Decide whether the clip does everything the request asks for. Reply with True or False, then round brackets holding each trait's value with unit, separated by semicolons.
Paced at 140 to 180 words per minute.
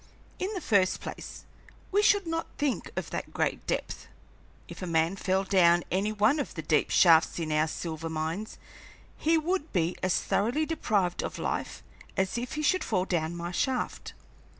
True (175 wpm)